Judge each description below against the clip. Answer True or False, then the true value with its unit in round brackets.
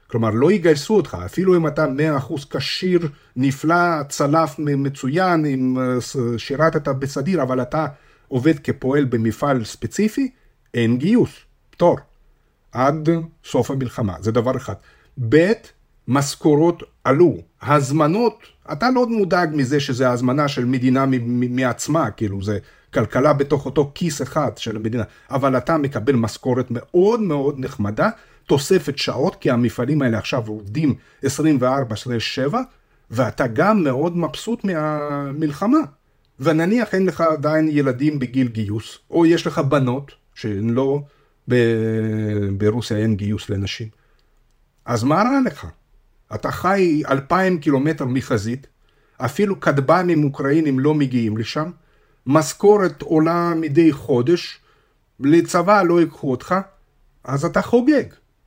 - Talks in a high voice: False (140 Hz)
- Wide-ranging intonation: False (4.7 semitones)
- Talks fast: False (125 wpm)